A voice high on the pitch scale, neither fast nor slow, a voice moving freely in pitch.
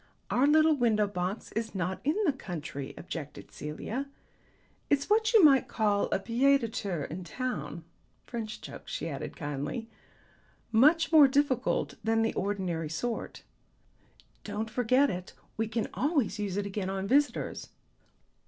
Yes: high, 220 Hz; average, 145 wpm; wide, 6.3 semitones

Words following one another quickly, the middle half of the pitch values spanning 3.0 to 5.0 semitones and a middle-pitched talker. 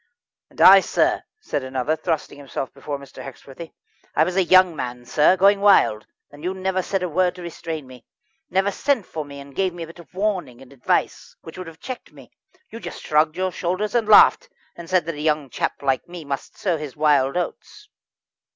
Yes: fast, 210 wpm; average, 4.7 semitones; medium, 165 Hz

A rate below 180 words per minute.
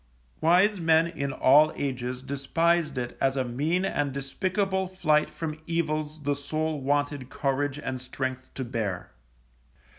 Yes: average, 140 wpm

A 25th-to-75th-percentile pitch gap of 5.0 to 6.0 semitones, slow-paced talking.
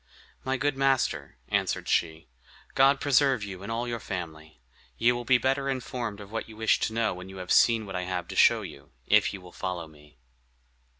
No: wide, 5.6 semitones; fast, 205 wpm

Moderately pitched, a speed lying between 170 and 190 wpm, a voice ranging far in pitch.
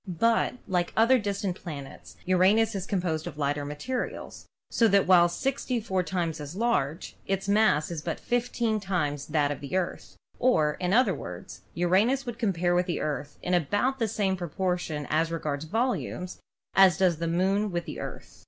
No: medium, 180 Hz; average, 175 wpm; average, 4.8 semitones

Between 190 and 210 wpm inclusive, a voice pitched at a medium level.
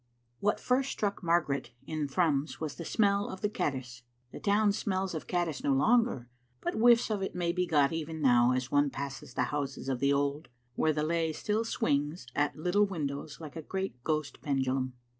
Yes: average, 195 wpm; medium, 155 Hz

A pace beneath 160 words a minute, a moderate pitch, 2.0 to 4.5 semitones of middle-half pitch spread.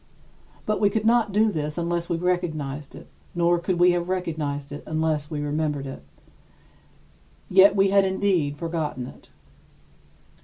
Yes: average, 150 wpm; medium, 170 Hz; average, 4.1 semitones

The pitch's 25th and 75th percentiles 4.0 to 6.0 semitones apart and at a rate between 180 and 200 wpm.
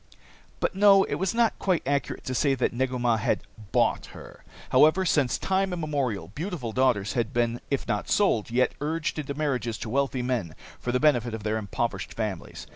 Yes: average, 4.8 semitones; average, 190 wpm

